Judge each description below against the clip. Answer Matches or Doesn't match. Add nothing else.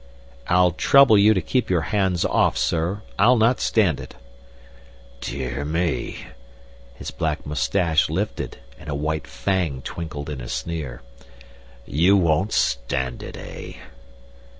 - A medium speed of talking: Doesn't match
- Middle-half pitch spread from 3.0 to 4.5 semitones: Doesn't match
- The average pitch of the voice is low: Matches